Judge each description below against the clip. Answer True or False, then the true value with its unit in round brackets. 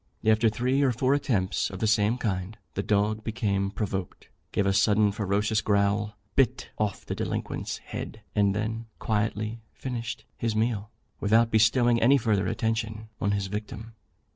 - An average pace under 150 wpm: False (155 wpm)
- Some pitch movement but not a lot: False (1.9 semitones)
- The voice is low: True (110 Hz)